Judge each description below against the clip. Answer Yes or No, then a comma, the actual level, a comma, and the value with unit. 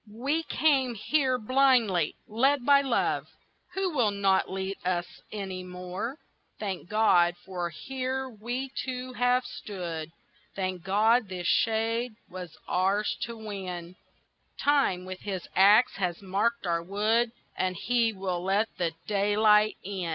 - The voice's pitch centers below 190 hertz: No, high, 210 Hz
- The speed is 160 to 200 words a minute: No, slow, 135 wpm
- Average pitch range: Yes, average, 4.9 semitones